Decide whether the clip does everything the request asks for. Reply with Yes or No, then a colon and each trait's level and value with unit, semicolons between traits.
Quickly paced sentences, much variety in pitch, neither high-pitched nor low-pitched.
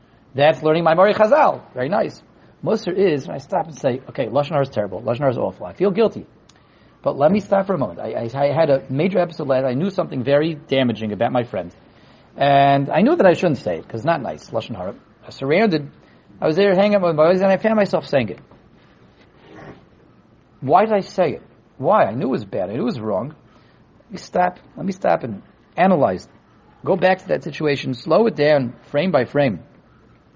Yes: fast, 220 wpm; wide, 5.9 semitones; medium, 155 Hz